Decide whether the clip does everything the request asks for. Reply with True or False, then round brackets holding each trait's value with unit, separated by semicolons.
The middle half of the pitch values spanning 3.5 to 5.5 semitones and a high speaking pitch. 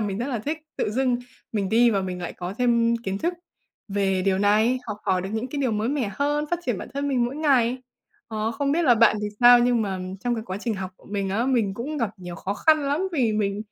True (4.4 semitones; 230 Hz)